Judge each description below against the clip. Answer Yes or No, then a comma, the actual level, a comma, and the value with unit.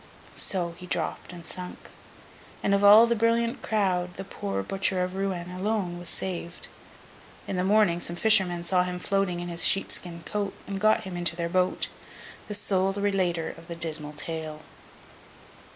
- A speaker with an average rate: Yes, average, 170 wpm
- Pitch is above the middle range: No, medium, 180 Hz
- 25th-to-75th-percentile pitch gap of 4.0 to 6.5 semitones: No, narrow, 2.4 semitones